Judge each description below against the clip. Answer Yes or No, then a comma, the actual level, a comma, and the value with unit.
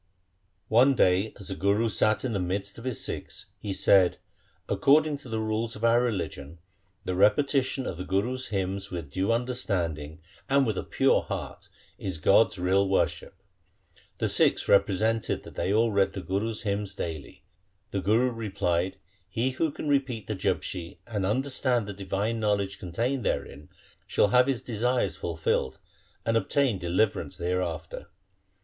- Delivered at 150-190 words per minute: Yes, average, 170 wpm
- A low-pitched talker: Yes, low, 105 Hz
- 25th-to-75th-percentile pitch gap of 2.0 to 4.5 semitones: Yes, average, 4.2 semitones